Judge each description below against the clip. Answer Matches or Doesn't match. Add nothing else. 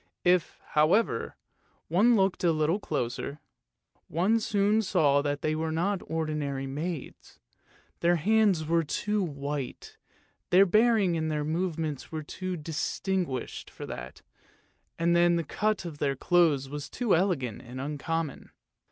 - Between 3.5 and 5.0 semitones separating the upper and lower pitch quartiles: Matches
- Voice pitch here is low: Doesn't match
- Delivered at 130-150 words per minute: Matches